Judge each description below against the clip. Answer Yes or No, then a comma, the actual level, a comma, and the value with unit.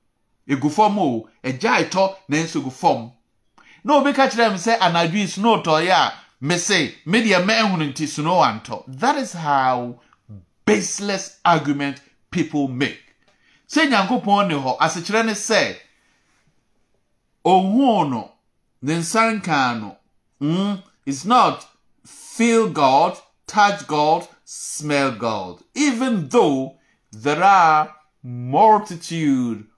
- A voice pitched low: No, medium, 165 Hz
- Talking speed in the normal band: No, slow, 115 wpm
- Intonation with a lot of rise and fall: Yes, wide, 7.2 semitones